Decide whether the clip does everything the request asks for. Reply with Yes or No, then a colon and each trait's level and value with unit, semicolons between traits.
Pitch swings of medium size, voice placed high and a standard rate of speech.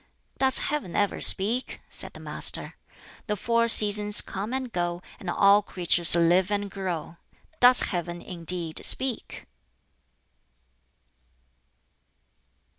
No: average, 4.4 semitones; high, 195 Hz; slow, 110 wpm